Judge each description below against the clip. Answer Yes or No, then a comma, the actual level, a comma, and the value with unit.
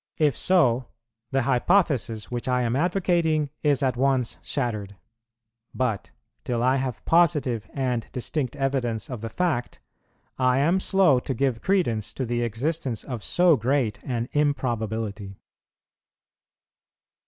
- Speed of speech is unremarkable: No, slow, 130 wpm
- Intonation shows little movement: No, average, 4.0 semitones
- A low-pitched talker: Yes, low, 130 Hz